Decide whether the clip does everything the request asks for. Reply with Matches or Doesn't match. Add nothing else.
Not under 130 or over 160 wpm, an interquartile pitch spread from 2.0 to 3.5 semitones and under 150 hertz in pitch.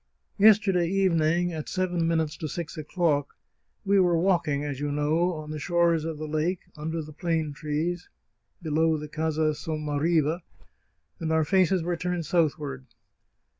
Doesn't match